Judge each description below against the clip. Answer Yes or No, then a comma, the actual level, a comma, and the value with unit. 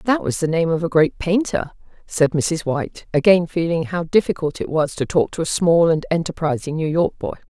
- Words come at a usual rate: No, fast, 215 wpm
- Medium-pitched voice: Yes, medium, 165 Hz